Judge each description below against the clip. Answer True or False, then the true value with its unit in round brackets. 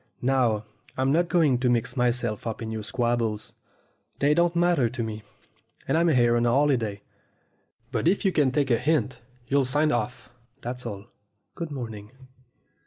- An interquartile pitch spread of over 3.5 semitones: True (4.2 semitones)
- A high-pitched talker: False (125 Hz)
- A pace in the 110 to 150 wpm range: False (170 wpm)